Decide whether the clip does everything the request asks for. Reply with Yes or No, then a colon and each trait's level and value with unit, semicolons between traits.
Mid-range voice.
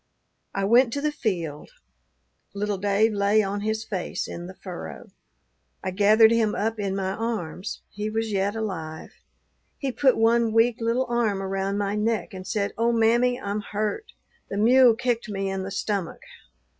No: high, 210 Hz